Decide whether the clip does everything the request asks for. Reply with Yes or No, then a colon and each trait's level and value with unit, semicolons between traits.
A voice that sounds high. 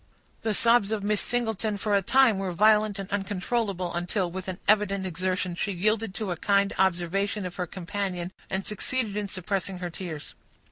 Yes: high, 195 Hz